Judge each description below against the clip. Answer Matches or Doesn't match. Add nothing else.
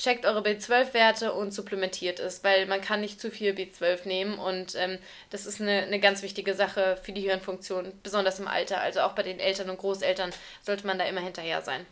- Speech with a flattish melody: Matches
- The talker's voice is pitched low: Doesn't match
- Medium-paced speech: Doesn't match